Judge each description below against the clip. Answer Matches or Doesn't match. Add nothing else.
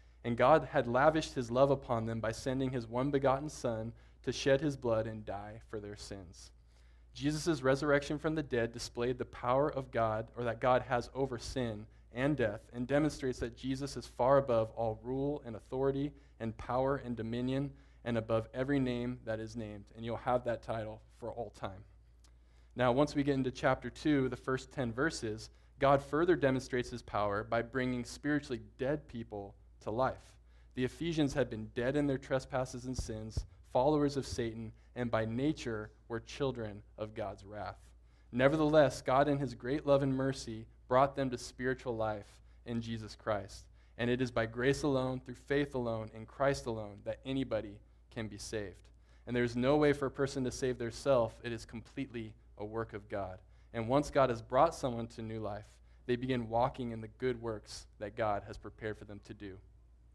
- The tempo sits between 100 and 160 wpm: Doesn't match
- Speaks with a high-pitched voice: Doesn't match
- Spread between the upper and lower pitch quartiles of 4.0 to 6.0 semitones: Doesn't match